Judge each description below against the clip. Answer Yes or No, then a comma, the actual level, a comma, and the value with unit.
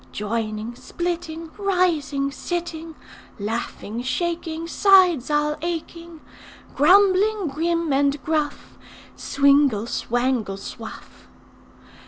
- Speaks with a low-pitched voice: No, very high, 310 Hz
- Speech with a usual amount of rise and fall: Yes, average, 4.7 semitones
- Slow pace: Yes, slow, 80 wpm